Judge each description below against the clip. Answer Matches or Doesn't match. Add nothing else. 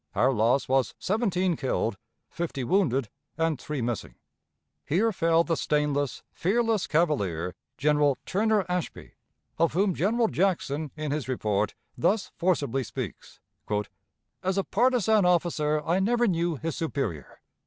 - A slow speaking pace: Matches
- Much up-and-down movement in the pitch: Matches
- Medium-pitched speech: Matches